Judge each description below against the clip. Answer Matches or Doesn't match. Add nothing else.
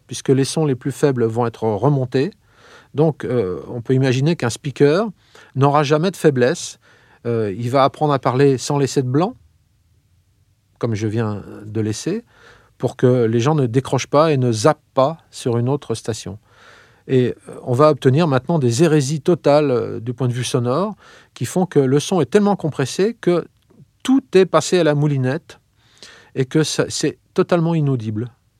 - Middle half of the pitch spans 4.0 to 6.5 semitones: Matches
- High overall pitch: Doesn't match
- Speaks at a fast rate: Doesn't match